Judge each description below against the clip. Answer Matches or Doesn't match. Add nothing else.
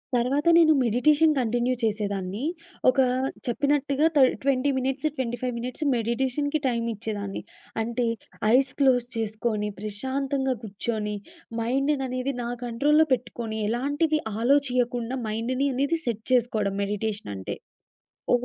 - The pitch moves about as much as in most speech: Matches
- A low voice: Doesn't match